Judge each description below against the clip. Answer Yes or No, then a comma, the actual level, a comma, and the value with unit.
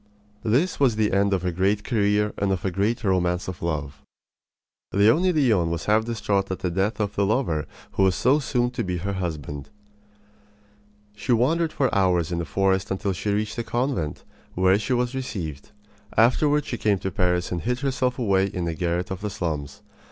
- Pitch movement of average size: Yes, average, 4.8 semitones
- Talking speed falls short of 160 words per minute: No, average, 195 wpm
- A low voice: Yes, low, 100 Hz